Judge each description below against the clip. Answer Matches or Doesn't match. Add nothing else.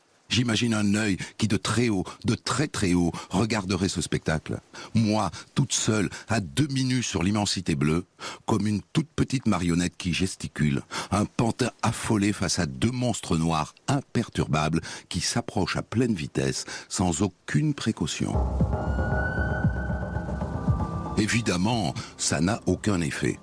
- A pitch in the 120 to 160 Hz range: Doesn't match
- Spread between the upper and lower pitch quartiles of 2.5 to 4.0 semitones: Doesn't match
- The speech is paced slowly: Matches